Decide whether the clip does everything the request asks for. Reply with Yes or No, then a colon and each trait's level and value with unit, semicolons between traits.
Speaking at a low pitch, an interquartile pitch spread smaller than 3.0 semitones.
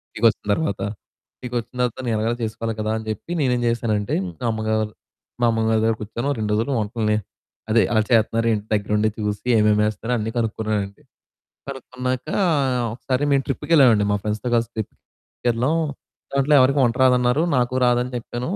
Yes: low, 115 Hz; narrow, 2.5 semitones